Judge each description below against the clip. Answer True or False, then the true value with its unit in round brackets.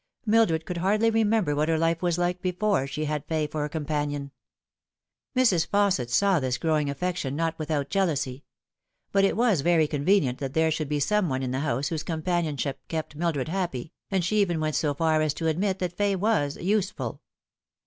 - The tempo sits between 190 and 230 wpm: True (195 wpm)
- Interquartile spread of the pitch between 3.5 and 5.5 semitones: True (4.3 semitones)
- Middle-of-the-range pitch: True (160 Hz)